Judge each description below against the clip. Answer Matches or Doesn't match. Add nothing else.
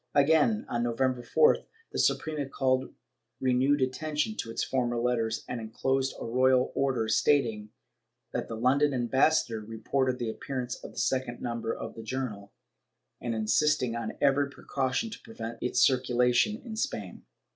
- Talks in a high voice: Doesn't match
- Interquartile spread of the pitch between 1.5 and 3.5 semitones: Matches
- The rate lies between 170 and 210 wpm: Doesn't match